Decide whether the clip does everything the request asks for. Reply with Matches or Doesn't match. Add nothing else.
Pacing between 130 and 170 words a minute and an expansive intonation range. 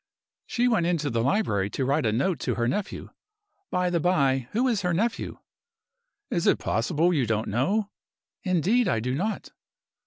Matches